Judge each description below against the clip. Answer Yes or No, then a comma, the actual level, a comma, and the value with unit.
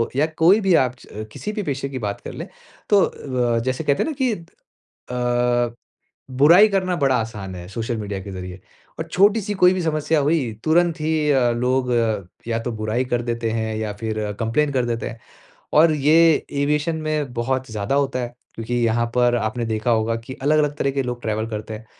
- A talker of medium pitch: No, low, 125 Hz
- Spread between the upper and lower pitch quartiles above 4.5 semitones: Yes, average, 5.1 semitones